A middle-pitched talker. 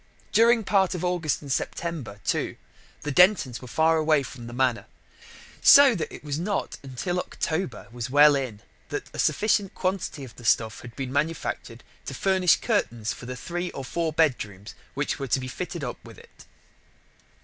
Yes: medium, 150 Hz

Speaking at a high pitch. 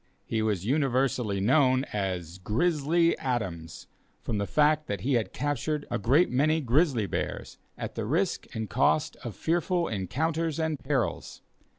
No: low, 130 Hz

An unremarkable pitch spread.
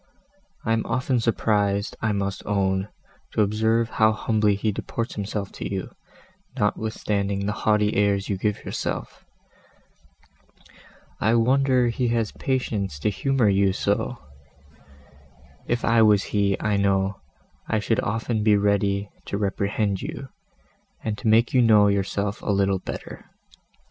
No: narrow, 2.1 semitones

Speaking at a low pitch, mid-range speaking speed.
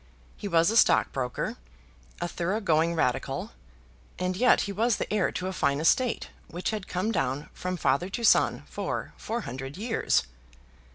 No: medium, 180 Hz; average, 165 wpm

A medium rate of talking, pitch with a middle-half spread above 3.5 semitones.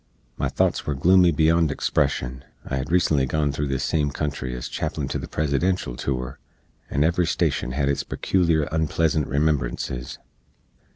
No: average, 155 wpm; average, 3.2 semitones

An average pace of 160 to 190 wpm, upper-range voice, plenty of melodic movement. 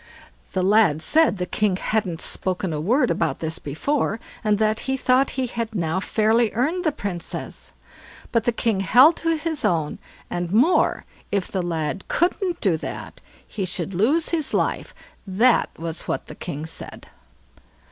Yes: average, 165 wpm; high, 210 Hz; wide, 6.5 semitones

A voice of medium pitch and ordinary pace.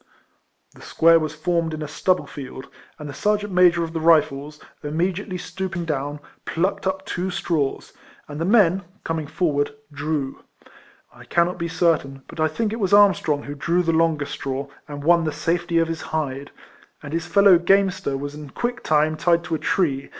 Yes: medium, 165 Hz; average, 190 wpm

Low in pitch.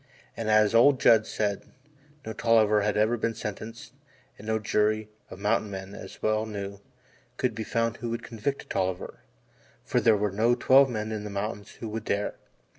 Yes: low, 110 Hz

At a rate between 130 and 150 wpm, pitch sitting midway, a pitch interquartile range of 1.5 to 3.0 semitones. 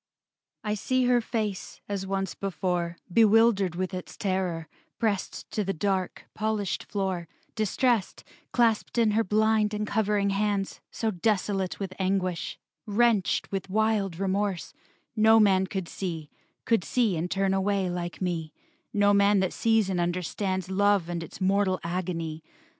No: average, 145 wpm; high, 195 Hz; narrow, 2.5 semitones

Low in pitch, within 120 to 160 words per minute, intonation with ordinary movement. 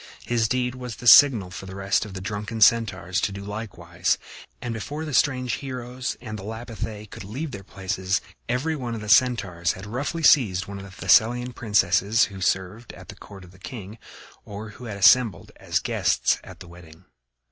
No: low, 105 Hz; average, 195 wpm; average, 4.2 semitones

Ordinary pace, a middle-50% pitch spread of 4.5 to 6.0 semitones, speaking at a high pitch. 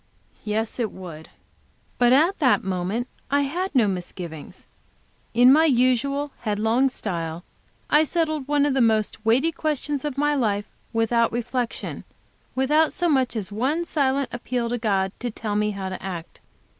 Yes: average, 155 wpm; average, 5.2 semitones; high, 245 Hz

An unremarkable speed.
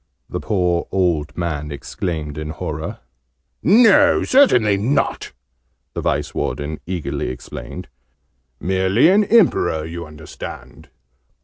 No: slow, 105 wpm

